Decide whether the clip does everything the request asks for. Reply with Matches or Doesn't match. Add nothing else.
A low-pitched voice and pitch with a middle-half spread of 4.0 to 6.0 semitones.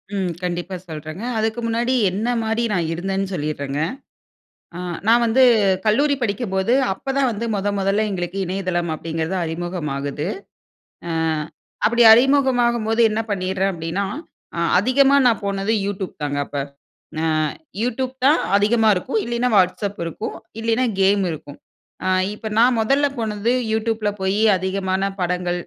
Doesn't match